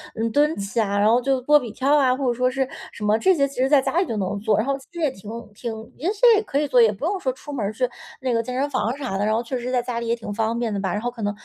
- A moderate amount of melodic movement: Yes, average, 3.9 semitones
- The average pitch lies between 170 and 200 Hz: No, high, 245 Hz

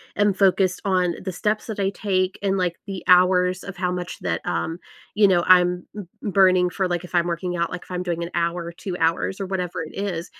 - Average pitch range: No, narrow, 1.6 semitones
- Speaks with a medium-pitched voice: Yes, medium, 180 Hz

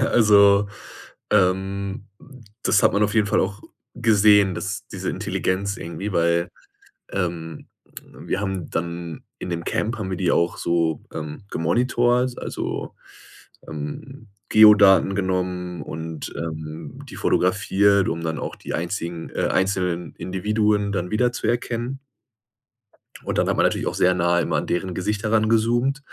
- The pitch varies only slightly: No, average, 3.5 semitones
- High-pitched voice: No, very low, 95 Hz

